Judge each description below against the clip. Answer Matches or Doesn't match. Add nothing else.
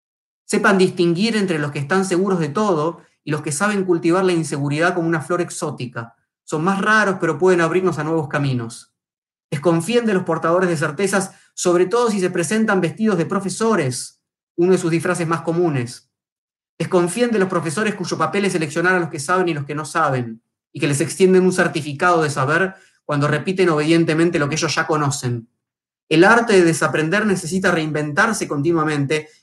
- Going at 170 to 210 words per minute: Matches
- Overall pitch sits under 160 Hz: Doesn't match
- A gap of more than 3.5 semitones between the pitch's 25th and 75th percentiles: Doesn't match